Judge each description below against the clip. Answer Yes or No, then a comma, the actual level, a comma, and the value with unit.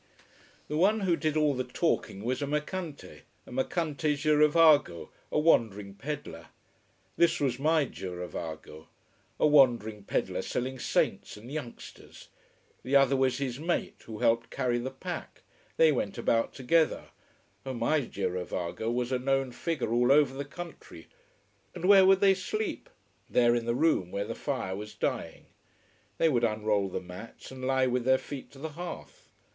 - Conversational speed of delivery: Yes, average, 160 wpm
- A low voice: Yes, low, 130 Hz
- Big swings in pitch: No, average, 4.7 semitones